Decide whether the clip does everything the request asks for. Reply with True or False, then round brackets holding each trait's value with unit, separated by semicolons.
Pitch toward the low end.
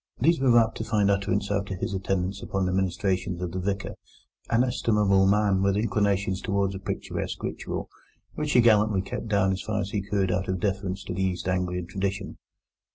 True (100 Hz)